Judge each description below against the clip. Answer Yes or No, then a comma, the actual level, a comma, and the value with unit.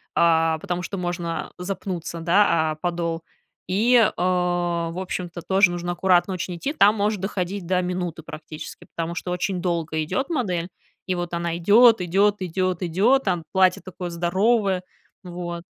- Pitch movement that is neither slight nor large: No, narrow, 2.0 semitones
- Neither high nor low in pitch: Yes, medium, 180 Hz